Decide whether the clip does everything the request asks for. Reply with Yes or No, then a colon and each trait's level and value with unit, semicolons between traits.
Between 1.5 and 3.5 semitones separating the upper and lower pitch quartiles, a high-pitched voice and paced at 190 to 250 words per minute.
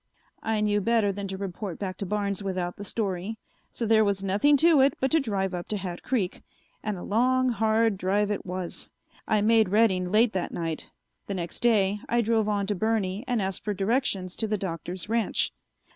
Yes: average, 2.9 semitones; high, 205 Hz; fast, 205 wpm